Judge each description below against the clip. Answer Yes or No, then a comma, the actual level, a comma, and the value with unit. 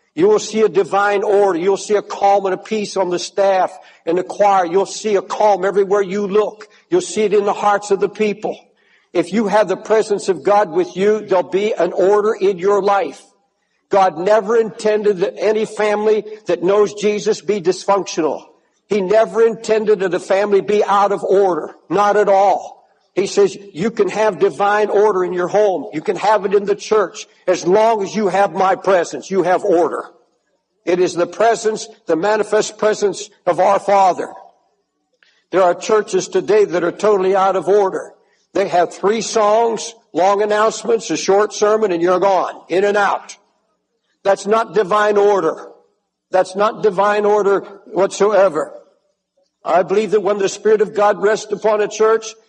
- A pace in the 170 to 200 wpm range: Yes, average, 180 wpm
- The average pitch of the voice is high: Yes, high, 205 Hz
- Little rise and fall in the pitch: Yes, narrow, 1.8 semitones